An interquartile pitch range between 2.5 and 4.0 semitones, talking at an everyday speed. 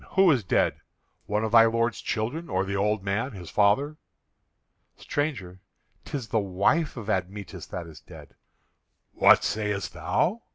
No: average, 4.6 semitones; average, 150 wpm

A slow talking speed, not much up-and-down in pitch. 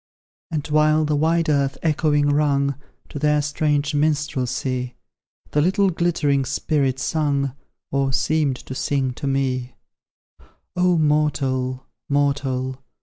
Yes: slow, 115 wpm; narrow, 2.2 semitones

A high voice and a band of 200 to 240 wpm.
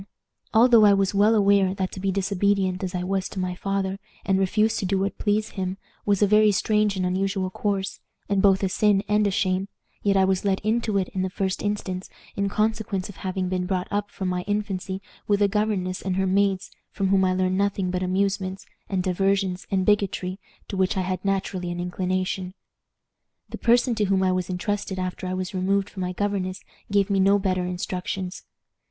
Yes: high, 195 Hz; fast, 205 wpm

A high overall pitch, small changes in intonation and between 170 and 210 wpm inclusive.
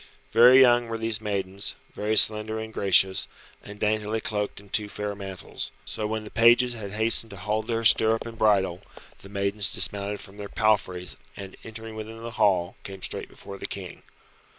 No: low, 105 Hz; narrow, 2.1 semitones; average, 180 wpm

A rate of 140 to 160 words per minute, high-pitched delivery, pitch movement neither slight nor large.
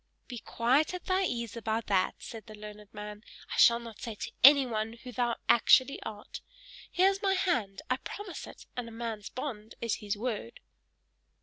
No: average, 185 wpm; high, 230 Hz; average, 3.5 semitones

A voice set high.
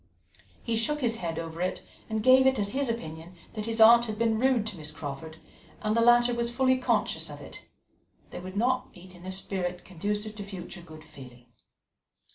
Yes: high, 210 Hz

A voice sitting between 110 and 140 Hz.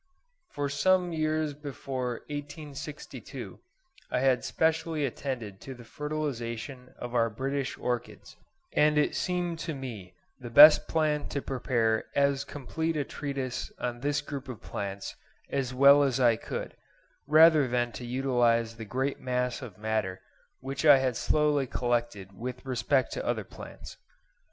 Yes: low, 135 Hz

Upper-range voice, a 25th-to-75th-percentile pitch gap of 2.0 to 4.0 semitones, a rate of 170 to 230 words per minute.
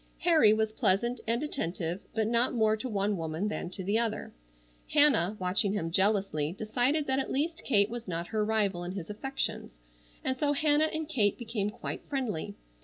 No: high, 215 Hz; average, 5.2 semitones; average, 180 wpm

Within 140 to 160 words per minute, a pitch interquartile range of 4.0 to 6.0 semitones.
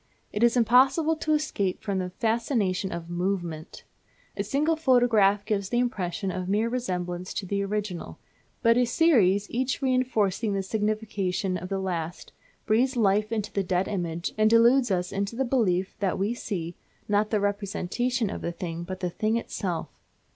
No: average, 170 wpm; average, 4.3 semitones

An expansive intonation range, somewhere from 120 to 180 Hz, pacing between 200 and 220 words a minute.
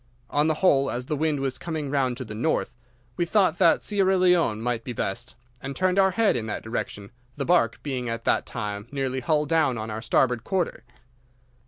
Yes: wide, 6.1 semitones; low, 135 Hz; fast, 205 wpm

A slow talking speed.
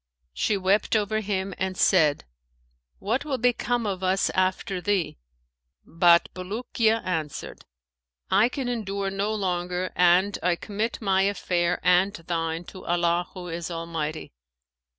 Yes: slow, 130 wpm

